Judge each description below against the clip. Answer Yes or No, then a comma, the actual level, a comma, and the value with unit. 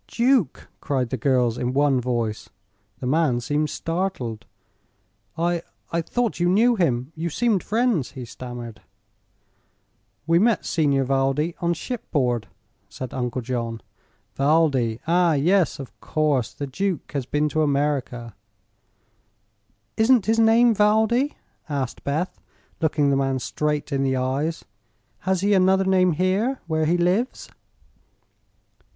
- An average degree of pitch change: No, wide, 6.2 semitones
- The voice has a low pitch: No, medium, 150 Hz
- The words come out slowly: Yes, slow, 130 wpm